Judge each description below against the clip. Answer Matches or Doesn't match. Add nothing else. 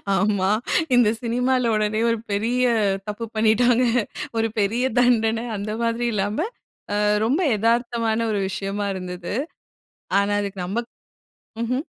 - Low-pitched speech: Doesn't match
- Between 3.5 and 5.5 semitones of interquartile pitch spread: Doesn't match